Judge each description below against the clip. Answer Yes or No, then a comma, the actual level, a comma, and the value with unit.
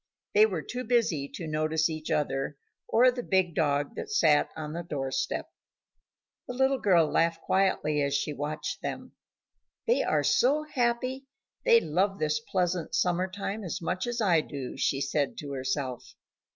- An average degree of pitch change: No, wide, 6.7 semitones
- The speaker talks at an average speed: Yes, average, 165 wpm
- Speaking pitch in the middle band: Yes, medium, 170 Hz